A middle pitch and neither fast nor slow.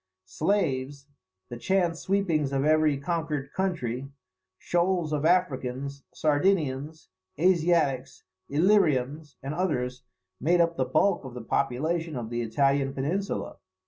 No: medium, 150 Hz; slow, 115 wpm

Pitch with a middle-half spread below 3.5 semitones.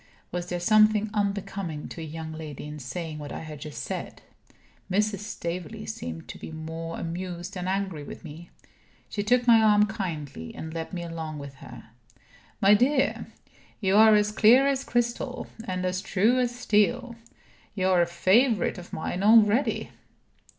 No: average, 4.8 semitones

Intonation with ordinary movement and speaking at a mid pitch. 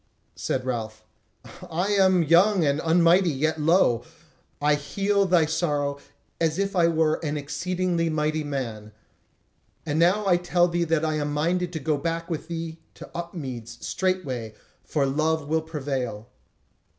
Yes: average, 3.1 semitones; medium, 160 Hz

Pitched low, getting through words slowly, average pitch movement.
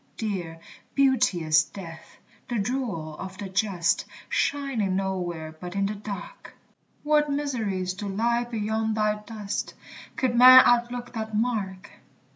No: high, 210 Hz; slow, 125 wpm; average, 4.4 semitones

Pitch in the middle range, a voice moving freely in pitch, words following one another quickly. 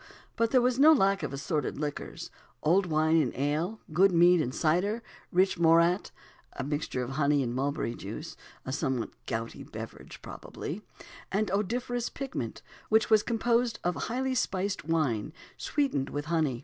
No: medium, 170 Hz; wide, 6.9 semitones; average, 155 wpm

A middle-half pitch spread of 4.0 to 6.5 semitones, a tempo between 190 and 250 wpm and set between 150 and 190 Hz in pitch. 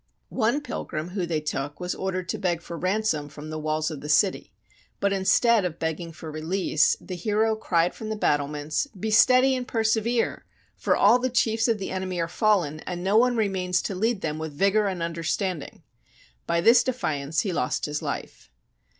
Yes: wide, 5.6 semitones; average, 195 wpm; medium, 185 Hz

